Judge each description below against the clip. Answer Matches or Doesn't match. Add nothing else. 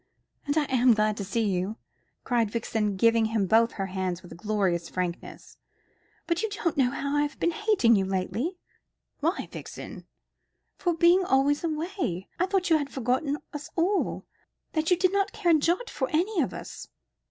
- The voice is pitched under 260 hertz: Doesn't match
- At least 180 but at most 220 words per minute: Matches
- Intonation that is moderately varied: Doesn't match